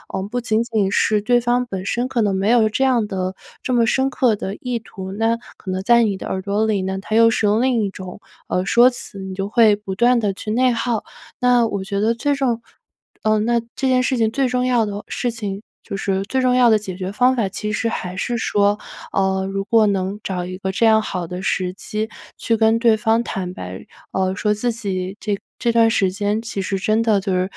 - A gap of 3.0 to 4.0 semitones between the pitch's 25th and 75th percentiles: Yes, average, 3.3 semitones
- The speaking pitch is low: No, high, 215 Hz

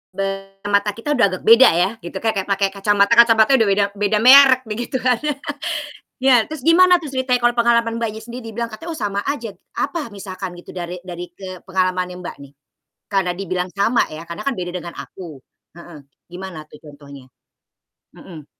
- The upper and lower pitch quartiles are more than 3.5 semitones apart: Yes, average, 4.6 semitones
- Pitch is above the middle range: Yes, high, 200 Hz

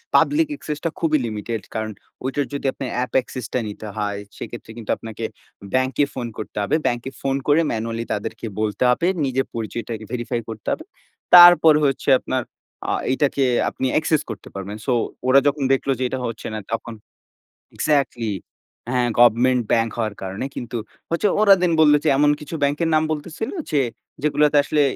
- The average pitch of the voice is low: Yes, low, 130 Hz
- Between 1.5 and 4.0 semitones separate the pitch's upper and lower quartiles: No, average, 4.5 semitones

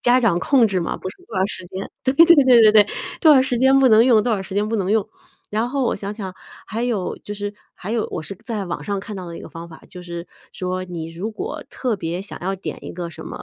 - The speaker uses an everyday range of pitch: Yes, average, 4.2 semitones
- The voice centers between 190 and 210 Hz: Yes, high, 205 Hz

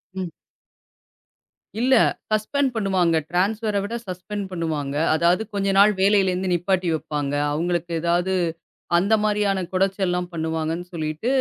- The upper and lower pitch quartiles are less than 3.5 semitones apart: Yes, average, 3.0 semitones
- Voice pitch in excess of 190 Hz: No, medium, 185 Hz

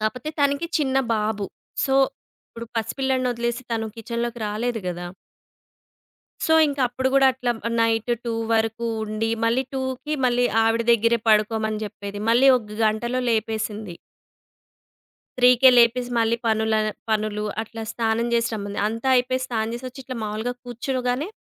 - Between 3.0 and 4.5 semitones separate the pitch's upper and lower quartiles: No, narrow, 2.4 semitones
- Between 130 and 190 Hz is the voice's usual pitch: No, high, 230 Hz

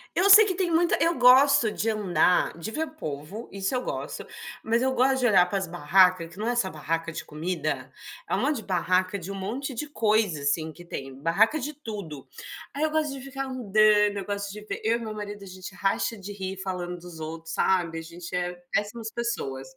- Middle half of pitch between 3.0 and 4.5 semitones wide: No, wide, 5.4 semitones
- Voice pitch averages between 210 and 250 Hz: No, high, 200 Hz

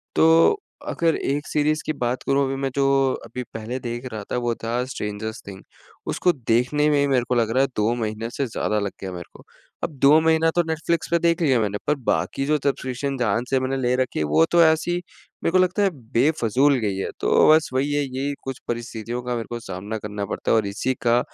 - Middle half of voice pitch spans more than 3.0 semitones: Yes, average, 4.4 semitones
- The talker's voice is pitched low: Yes, low, 125 Hz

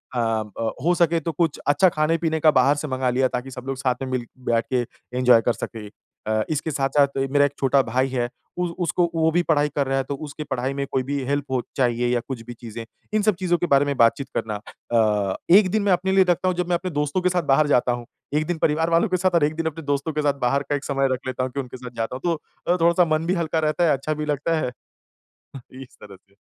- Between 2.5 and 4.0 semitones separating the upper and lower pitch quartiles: No, average, 4.4 semitones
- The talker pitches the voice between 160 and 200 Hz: No, medium, 140 Hz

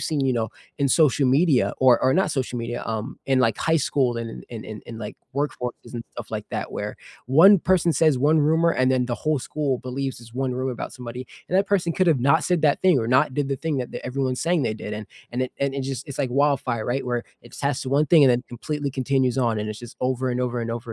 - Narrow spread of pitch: No, average, 3.3 semitones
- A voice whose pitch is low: Yes, low, 130 Hz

